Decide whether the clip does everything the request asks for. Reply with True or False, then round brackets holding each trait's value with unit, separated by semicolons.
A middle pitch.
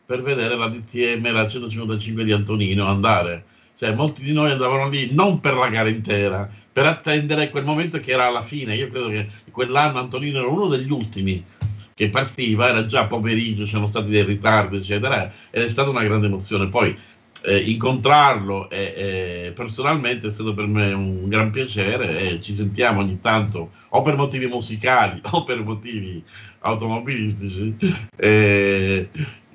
False (110 Hz)